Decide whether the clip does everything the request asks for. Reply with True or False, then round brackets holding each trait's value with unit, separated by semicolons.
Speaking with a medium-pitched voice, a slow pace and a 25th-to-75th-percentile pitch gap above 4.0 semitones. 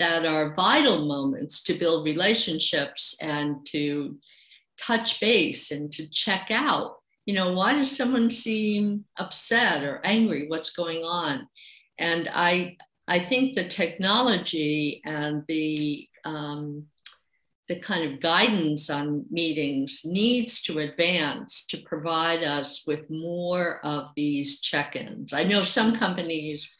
True (165 Hz; 130 wpm; 4.5 semitones)